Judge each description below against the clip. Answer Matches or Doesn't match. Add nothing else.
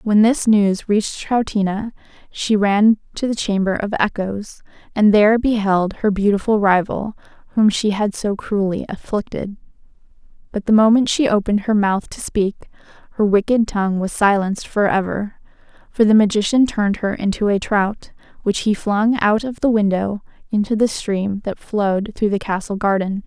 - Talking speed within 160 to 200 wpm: Matches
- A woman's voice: Matches